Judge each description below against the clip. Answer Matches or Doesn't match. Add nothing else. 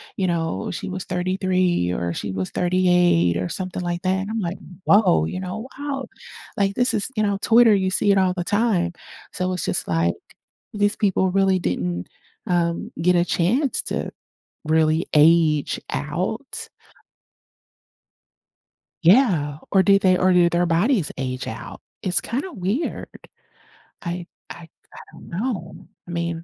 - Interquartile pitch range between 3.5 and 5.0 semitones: Doesn't match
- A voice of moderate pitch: Matches